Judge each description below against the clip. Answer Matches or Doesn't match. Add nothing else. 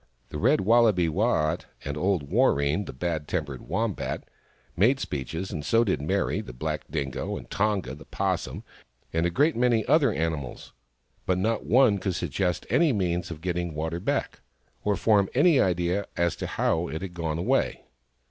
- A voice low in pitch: Matches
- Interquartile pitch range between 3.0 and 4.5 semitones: Doesn't match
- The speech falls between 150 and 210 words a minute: Matches